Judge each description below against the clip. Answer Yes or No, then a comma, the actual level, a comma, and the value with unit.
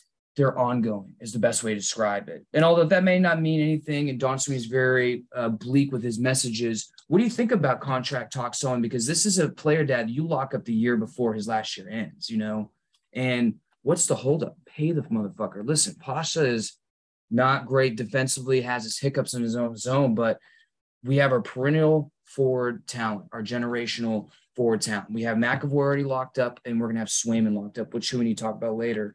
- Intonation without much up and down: No, average, 3.4 semitones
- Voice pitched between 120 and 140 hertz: Yes, low, 125 Hz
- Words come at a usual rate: No, fast, 215 wpm